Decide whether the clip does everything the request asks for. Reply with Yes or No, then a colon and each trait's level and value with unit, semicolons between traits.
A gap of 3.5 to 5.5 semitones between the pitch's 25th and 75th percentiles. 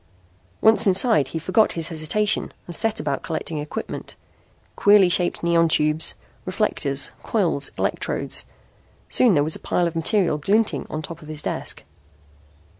Yes: average, 4.8 semitones